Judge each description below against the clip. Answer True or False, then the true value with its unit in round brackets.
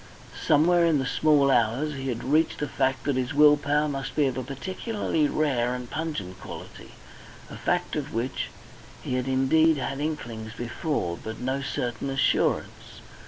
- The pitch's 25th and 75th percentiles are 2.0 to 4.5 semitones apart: True (3.3 semitones)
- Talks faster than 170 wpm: False (165 wpm)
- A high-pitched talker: False (135 Hz)